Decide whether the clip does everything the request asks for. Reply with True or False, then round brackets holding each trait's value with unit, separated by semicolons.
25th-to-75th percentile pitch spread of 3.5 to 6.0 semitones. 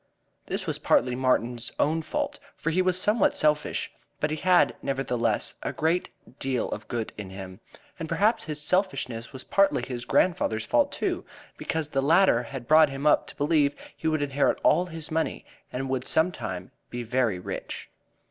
True (4.9 semitones)